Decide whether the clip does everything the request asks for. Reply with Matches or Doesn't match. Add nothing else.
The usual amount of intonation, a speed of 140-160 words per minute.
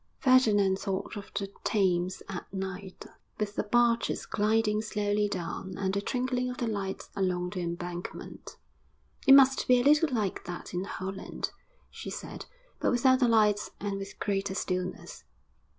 Matches